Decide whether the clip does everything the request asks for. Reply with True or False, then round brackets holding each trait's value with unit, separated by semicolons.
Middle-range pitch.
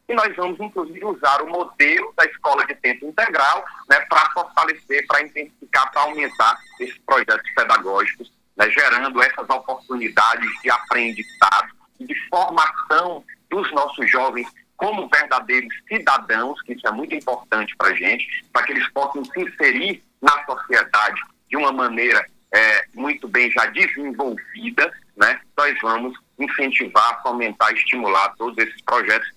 True (155 Hz)